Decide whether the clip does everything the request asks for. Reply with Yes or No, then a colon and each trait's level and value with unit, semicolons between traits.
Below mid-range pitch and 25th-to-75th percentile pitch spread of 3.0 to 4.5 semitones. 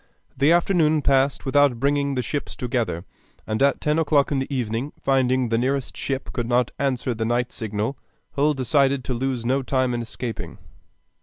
No: low, 130 Hz; narrow, 2.5 semitones